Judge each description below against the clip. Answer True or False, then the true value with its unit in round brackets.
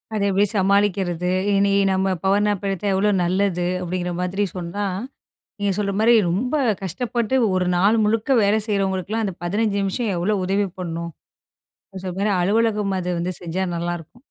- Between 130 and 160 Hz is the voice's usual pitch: False (195 Hz)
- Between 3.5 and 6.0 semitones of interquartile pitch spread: False (2.5 semitones)